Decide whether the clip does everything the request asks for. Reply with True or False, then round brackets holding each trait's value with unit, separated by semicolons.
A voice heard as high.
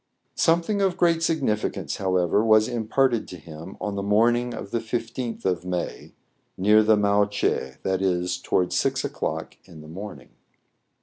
False (105 Hz)